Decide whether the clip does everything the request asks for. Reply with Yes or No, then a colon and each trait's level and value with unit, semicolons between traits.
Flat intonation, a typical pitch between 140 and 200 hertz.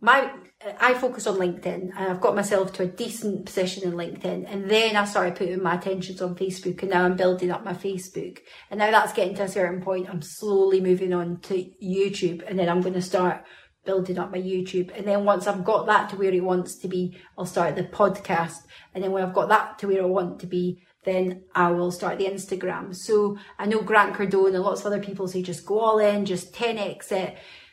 Yes: narrow, 1.8 semitones; high, 190 Hz